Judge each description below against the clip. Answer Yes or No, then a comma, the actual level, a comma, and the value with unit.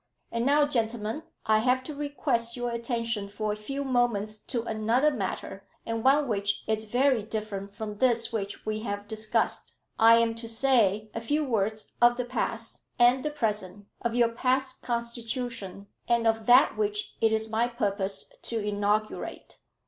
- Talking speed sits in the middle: Yes, average, 165 wpm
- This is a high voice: Yes, high, 230 Hz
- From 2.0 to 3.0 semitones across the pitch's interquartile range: Yes, narrow, 2.5 semitones